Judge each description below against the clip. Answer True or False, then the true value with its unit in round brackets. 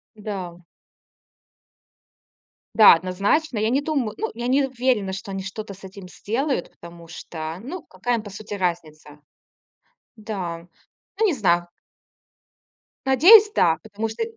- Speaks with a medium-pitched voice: False (205 Hz)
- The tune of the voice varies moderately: False (5.9 semitones)